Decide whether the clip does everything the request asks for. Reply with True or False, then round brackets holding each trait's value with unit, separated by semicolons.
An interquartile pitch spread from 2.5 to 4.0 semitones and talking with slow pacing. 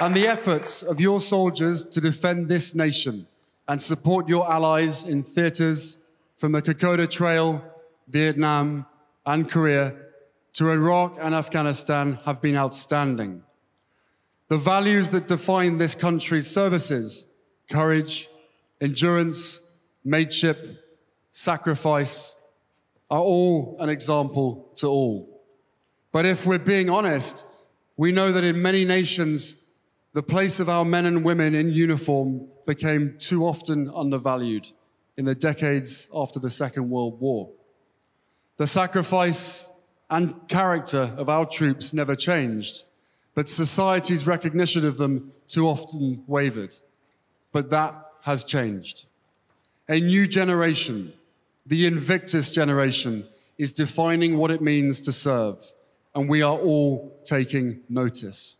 True (3.3 semitones; 120 wpm)